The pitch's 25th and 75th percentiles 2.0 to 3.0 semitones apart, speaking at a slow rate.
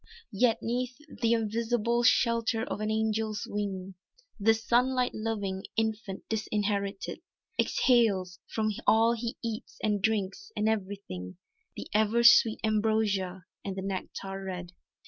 Yes: narrow, 2.6 semitones; slow, 125 wpm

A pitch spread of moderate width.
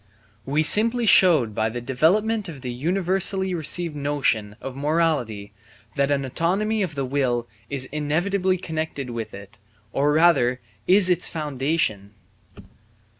No: wide, 5.9 semitones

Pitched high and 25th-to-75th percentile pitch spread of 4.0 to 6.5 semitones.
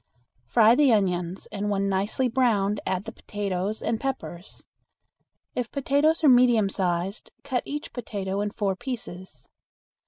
Yes: high, 210 Hz; average, 4.4 semitones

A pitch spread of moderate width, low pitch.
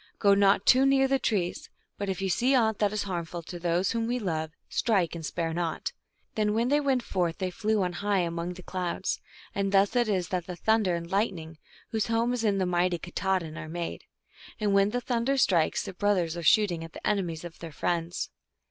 No: average, 3.9 semitones; high, 190 Hz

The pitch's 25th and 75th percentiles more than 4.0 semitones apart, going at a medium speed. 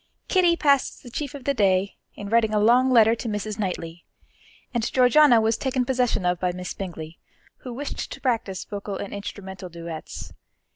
Yes: average, 4.9 semitones; average, 180 wpm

